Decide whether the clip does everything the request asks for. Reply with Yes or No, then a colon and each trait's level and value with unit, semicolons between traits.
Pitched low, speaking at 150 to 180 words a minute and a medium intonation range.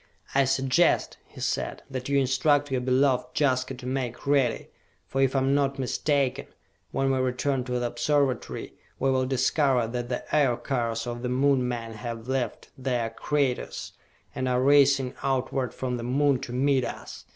No: low, 130 Hz; average, 170 wpm; narrow, 1.7 semitones